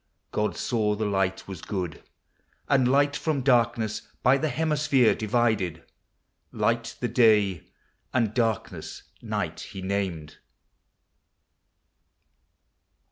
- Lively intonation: No, average, 4.2 semitones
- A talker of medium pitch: No, low, 110 Hz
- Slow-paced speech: Yes, slow, 100 wpm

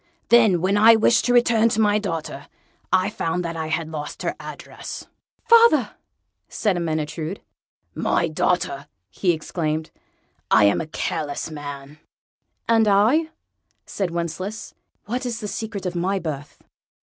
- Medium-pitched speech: Yes, medium, 180 Hz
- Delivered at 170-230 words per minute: No, average, 140 wpm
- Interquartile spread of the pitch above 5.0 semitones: Yes, wide, 5.6 semitones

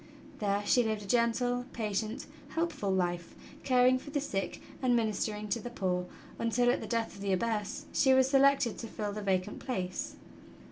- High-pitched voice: Yes, high, 225 Hz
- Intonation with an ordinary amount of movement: Yes, average, 3.8 semitones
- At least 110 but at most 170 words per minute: No, average, 180 wpm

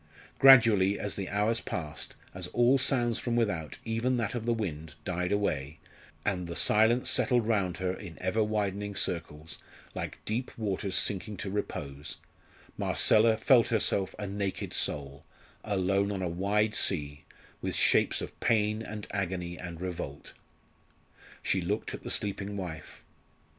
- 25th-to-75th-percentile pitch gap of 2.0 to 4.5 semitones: Yes, average, 3.5 semitones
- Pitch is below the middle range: Yes, low, 100 Hz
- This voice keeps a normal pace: Yes, average, 150 wpm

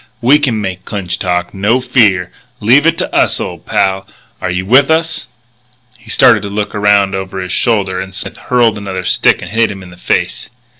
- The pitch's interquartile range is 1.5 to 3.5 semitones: No, average, 3.9 semitones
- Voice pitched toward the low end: Yes, low, 100 Hz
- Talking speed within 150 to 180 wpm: No, average, 200 wpm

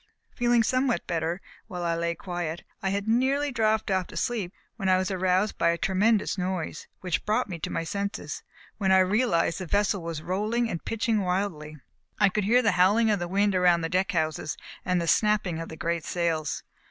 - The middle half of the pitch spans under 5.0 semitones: Yes, average, 3.8 semitones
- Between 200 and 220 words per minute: Yes, fast, 205 wpm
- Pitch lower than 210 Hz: Yes, high, 190 Hz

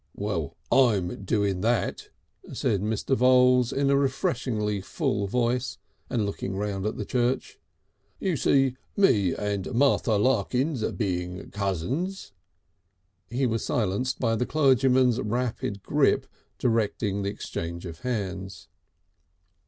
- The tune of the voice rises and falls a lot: No, average, 4.5 semitones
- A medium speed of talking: No, slow, 120 wpm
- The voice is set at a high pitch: No, low, 110 Hz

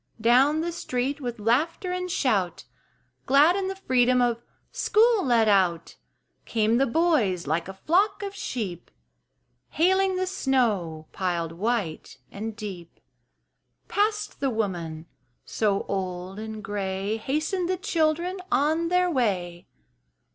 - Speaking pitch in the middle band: No, high, 240 Hz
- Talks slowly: Yes, slow, 125 wpm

